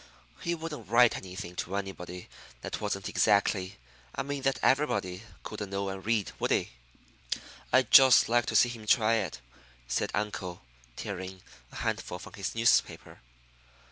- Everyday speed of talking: Yes, average, 150 wpm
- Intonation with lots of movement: No, average, 4.4 semitones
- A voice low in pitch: Yes, low, 105 Hz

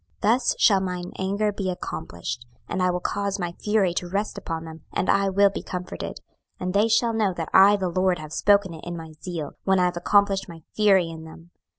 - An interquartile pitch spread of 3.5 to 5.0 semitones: No, average, 2.7 semitones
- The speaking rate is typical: No, fast, 225 wpm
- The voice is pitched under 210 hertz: Yes, medium, 185 Hz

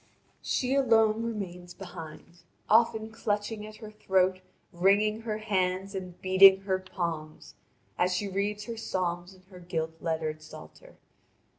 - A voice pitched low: No, high, 190 Hz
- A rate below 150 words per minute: Yes, slow, 135 wpm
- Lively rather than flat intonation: No, average, 3.2 semitones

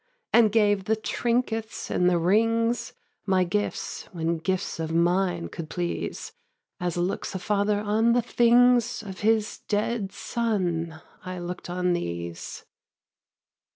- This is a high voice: Yes, high, 195 Hz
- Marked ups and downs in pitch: No, average, 4.2 semitones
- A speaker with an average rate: No, slow, 130 wpm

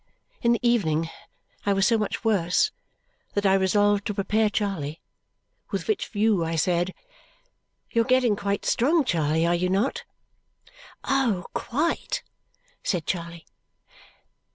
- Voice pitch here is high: Yes, high, 200 Hz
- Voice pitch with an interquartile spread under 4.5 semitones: No, average, 4.8 semitones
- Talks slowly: Yes, slow, 130 wpm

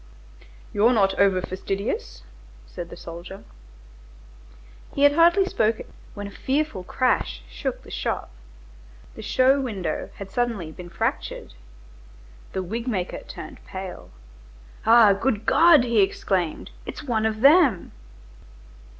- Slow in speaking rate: Yes, slow, 125 wpm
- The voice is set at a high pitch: Yes, high, 210 Hz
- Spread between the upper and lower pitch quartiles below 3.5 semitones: No, wide, 5.4 semitones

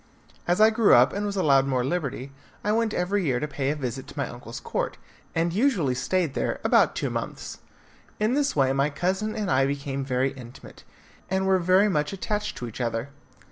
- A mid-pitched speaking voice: Yes, medium, 150 Hz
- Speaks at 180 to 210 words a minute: Yes, average, 200 wpm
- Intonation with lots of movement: Yes, wide, 6.9 semitones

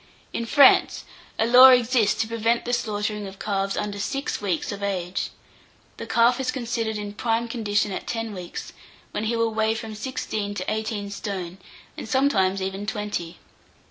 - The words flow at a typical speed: Yes, average, 170 wpm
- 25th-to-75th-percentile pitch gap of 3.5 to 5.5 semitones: No, narrow, 2.4 semitones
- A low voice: No, high, 215 Hz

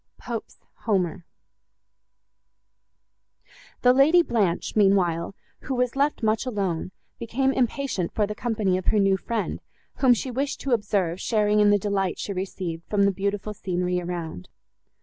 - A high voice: Yes, high, 205 Hz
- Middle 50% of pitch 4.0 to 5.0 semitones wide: Yes, average, 4.4 semitones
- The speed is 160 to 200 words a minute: No, average, 145 wpm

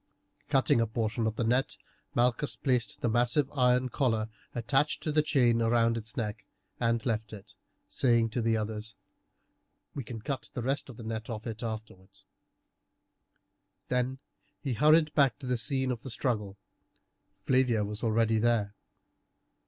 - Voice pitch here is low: Yes, low, 115 Hz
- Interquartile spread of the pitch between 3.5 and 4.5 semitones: No, narrow, 2.6 semitones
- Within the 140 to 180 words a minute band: Yes, average, 160 wpm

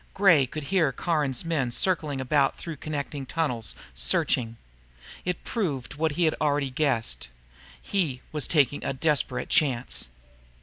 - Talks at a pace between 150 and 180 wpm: No, slow, 135 wpm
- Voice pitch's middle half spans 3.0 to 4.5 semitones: Yes, average, 3.5 semitones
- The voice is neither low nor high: Yes, medium, 145 Hz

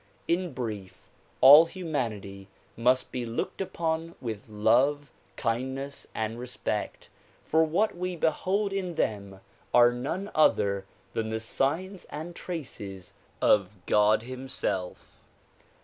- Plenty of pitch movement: Yes, wide, 7.1 semitones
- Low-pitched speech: Yes, low, 130 Hz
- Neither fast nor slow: No, slow, 115 wpm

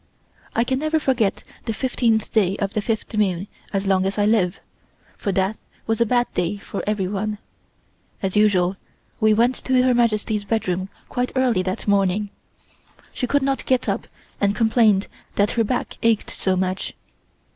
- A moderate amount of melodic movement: Yes, average, 3.3 semitones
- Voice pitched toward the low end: No, high, 210 Hz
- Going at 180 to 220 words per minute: No, average, 165 wpm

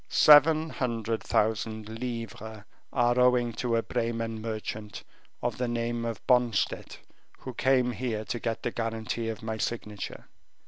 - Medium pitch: No, low, 115 Hz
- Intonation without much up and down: Yes, narrow, 1.8 semitones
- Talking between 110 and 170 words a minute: Yes, average, 140 wpm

